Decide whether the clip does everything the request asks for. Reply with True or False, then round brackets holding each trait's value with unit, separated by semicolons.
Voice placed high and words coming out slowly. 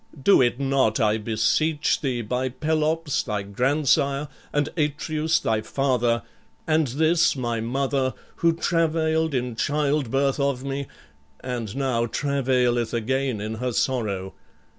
False (135 Hz; 125 wpm)